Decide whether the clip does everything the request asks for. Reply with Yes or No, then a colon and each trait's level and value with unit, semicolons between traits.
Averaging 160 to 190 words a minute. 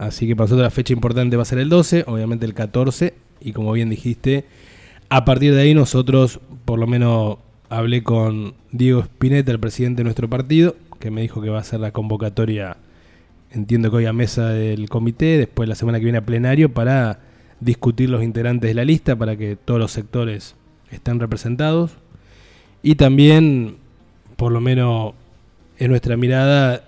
Yes: average, 180 wpm